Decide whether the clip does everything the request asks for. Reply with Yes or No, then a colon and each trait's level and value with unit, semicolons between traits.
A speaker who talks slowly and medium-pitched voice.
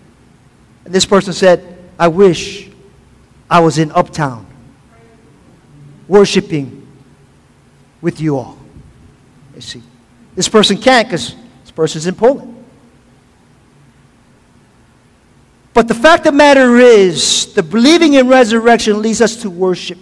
Yes: slow, 120 wpm; medium, 180 Hz